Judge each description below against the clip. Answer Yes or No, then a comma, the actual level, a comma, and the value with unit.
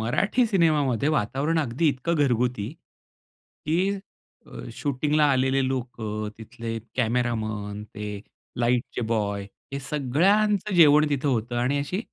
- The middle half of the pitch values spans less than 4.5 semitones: No, average, 4.9 semitones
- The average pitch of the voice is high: No, low, 130 Hz